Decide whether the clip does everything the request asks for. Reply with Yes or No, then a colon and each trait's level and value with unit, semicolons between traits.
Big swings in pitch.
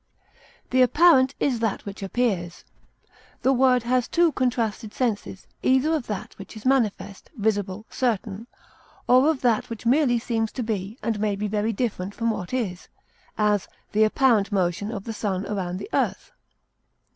No: average, 3.8 semitones